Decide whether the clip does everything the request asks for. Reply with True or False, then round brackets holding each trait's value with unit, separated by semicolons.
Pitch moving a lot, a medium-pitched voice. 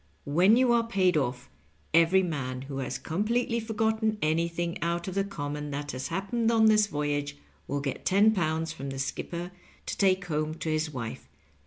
True (6.0 semitones; 170 Hz)